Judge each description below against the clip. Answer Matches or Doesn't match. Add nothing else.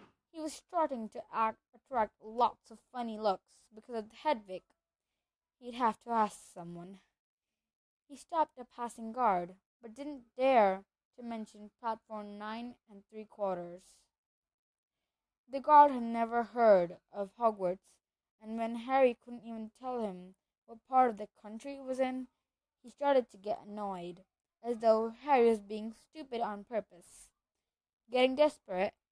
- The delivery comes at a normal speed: Matches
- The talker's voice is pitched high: Matches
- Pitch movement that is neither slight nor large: Matches